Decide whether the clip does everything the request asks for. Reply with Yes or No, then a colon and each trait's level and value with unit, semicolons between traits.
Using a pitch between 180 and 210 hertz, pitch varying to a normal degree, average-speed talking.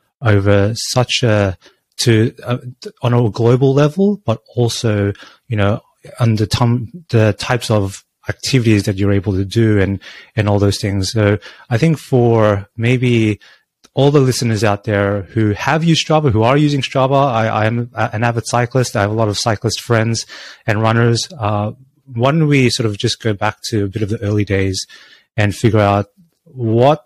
No: low, 115 Hz; average, 3.2 semitones; average, 180 wpm